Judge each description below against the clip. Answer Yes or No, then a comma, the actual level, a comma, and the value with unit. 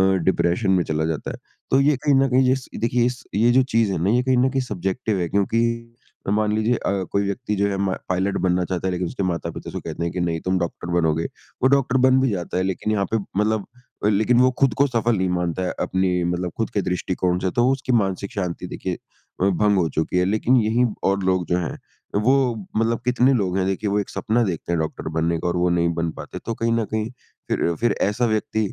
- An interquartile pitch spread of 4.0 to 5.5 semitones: Yes, average, 4.6 semitones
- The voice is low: Yes, low, 100 Hz